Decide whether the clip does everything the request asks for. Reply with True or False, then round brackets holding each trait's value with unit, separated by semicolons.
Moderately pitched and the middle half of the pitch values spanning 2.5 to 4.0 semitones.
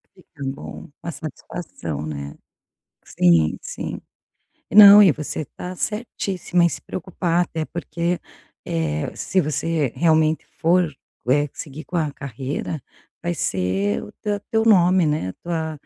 False (160 Hz; 4.8 semitones)